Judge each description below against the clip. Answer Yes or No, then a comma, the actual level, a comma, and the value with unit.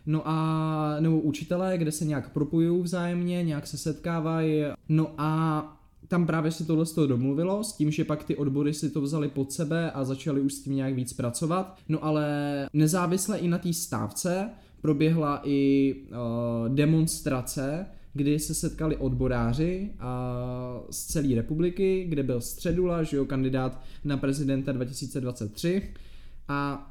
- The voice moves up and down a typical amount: Yes, average, 3.1 semitones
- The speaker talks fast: No, average, 150 wpm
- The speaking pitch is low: No, medium, 150 Hz